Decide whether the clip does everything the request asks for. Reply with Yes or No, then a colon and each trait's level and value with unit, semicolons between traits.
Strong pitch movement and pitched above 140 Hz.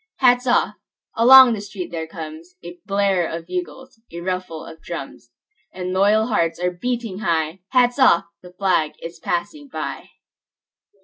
Yes: wide, 6.0 semitones; medium, 185 Hz